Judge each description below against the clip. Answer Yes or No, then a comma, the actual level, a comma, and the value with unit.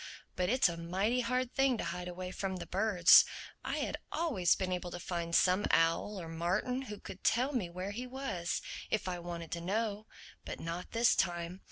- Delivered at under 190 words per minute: No, average, 195 wpm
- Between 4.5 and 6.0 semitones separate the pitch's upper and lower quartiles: Yes, average, 4.8 semitones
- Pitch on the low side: No, medium, 185 Hz